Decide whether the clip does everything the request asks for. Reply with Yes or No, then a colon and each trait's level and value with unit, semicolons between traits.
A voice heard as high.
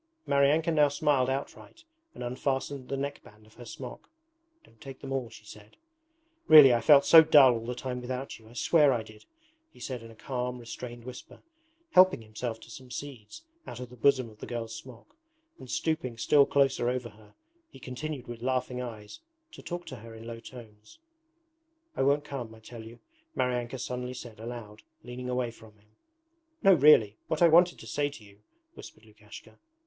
No: low, 125 Hz